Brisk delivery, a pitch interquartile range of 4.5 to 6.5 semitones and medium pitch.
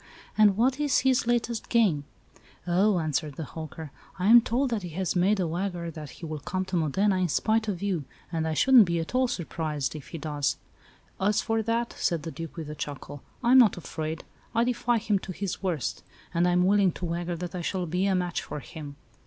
Yes: fast, 225 wpm; average, 4.9 semitones; medium, 180 Hz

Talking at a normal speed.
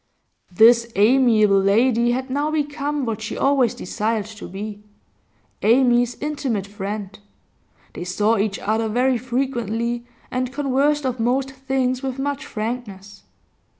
No: slow, 125 wpm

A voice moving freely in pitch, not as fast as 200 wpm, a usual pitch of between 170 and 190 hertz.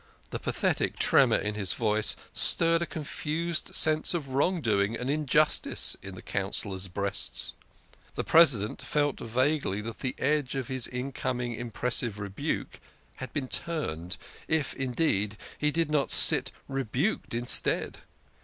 No: wide, 6.3 semitones; slow, 135 wpm; low, 130 Hz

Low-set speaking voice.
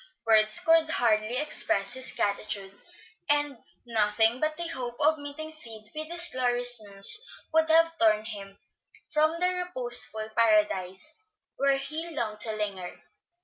No: high, 245 Hz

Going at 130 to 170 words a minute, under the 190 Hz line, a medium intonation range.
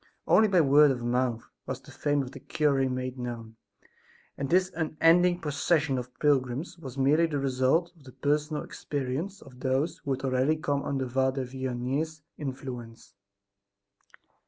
Yes: average, 155 wpm; low, 135 Hz; average, 3.1 semitones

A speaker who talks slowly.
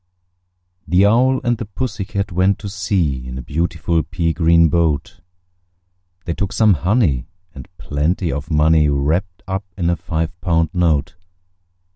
No: average, 150 wpm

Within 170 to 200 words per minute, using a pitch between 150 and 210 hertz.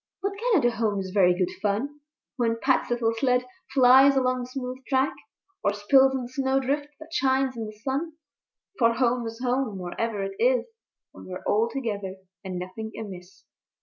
No: average, 175 wpm; high, 245 Hz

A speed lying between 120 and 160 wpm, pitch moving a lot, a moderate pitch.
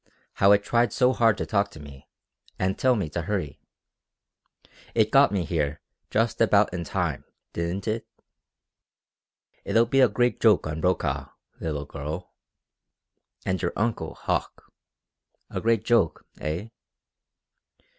No: slow, 135 wpm; wide, 6.0 semitones; low, 100 Hz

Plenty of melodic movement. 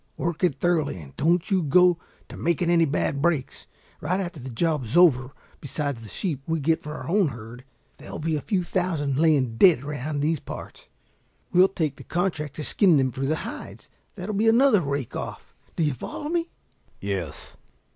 No: average, 4.4 semitones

